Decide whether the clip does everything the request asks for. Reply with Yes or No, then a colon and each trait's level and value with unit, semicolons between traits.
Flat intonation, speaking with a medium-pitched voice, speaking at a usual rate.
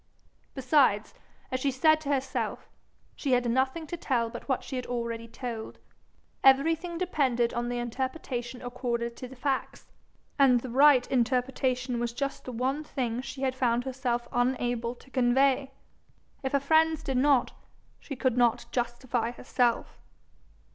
No: narrow, 2.2 semitones; very high, 255 Hz; average, 150 wpm